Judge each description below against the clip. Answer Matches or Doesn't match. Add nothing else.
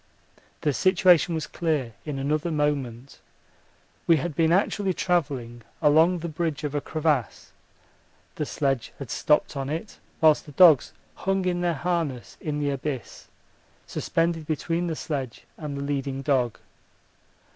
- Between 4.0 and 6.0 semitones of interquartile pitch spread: Doesn't match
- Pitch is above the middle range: Doesn't match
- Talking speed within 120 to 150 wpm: Matches